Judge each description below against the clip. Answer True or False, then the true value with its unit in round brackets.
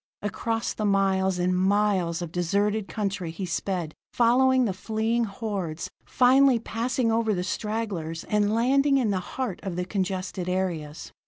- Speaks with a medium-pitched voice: False (200 Hz)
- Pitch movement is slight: False (3.8 semitones)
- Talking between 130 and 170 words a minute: True (150 wpm)